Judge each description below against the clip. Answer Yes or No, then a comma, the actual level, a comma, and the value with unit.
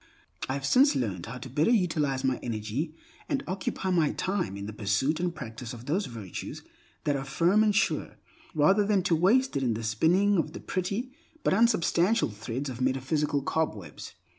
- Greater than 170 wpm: Yes, average, 185 wpm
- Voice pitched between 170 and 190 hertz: No, medium, 150 Hz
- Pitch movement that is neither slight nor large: No, wide, 7.6 semitones